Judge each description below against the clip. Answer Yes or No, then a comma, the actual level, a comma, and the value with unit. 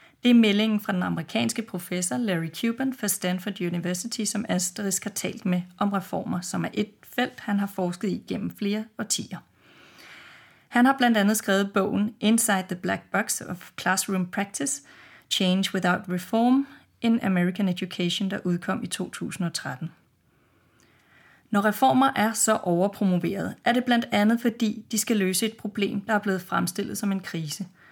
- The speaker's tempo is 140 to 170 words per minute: Yes, average, 160 wpm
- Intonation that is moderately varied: Yes, average, 3.4 semitones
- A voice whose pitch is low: No, high, 205 Hz